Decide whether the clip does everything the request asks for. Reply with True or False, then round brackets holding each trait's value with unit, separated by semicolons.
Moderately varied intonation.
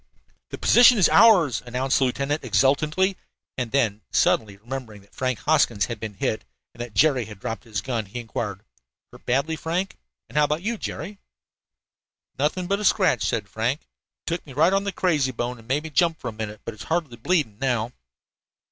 False (6.2 semitones)